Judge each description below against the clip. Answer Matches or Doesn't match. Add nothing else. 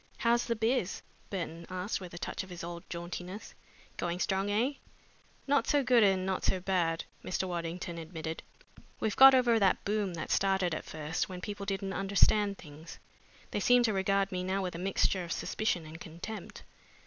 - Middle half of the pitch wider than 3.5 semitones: Doesn't match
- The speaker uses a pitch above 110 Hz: Matches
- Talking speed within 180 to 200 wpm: Matches